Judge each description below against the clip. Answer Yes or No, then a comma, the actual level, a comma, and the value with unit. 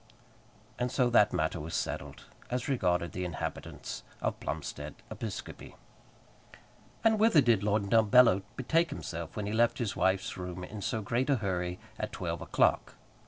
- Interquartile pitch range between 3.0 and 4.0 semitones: No, average, 5.2 semitones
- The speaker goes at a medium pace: Yes, average, 155 wpm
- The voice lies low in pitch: Yes, low, 105 Hz